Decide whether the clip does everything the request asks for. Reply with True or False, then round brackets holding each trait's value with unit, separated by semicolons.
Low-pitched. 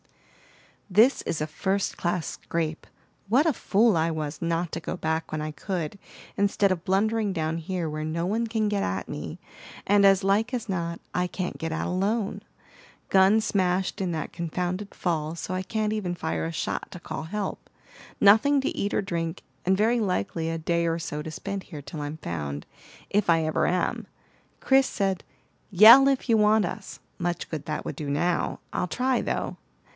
False (180 Hz)